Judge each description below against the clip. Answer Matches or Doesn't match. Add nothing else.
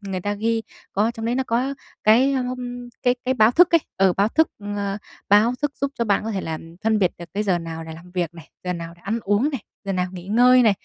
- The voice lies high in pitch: Matches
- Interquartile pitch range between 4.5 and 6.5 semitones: Matches